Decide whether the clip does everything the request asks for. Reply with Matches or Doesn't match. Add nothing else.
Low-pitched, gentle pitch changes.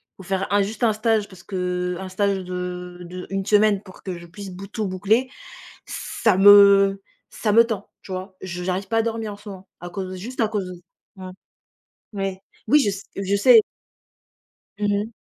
Doesn't match